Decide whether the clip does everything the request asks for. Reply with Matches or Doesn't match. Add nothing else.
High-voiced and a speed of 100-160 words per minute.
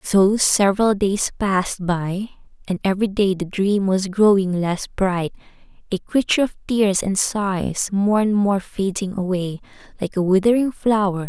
Matches